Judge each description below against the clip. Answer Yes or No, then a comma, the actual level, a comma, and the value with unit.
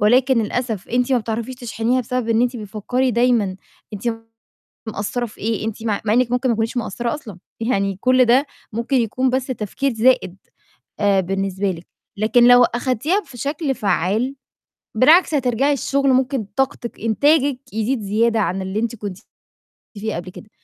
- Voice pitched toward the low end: No, high, 235 Hz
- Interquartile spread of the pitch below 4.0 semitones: Yes, average, 3.3 semitones